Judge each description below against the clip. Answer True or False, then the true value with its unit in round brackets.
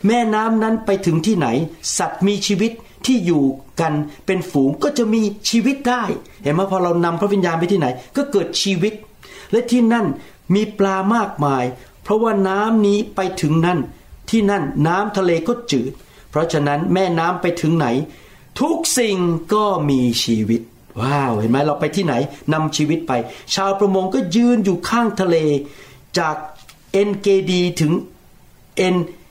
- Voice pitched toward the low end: False (185 Hz)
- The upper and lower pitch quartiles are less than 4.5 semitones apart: False (5.6 semitones)